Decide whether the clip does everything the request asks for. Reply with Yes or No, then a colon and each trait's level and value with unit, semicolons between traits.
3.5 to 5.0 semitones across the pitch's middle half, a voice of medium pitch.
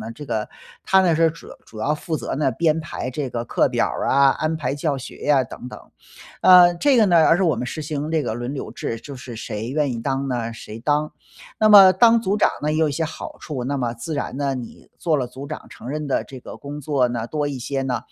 Yes: average, 4.0 semitones; medium, 145 Hz